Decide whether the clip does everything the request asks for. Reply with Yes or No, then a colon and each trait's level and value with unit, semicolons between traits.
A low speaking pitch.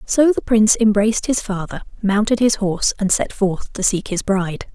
No: high, 205 Hz